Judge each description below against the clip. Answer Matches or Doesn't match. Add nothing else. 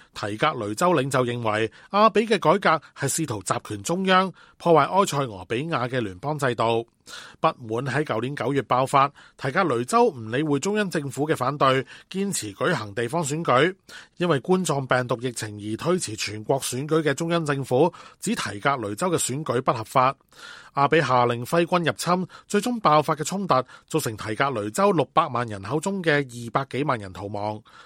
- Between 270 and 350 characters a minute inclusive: Matches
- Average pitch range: Doesn't match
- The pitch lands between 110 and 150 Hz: Matches